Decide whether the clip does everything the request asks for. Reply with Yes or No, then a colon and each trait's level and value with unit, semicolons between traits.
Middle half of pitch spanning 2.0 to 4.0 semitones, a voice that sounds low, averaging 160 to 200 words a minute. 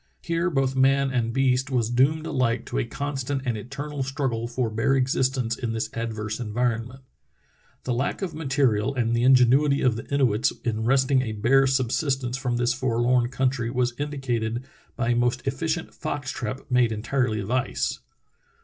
Yes: narrow, 2.5 semitones; low, 130 Hz; average, 170 wpm